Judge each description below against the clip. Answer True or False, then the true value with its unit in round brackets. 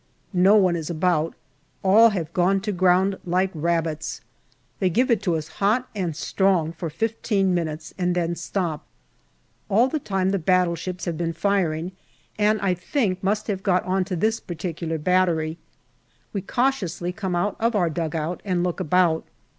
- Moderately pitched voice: True (180 Hz)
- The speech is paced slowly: False (160 wpm)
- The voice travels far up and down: False (2.8 semitones)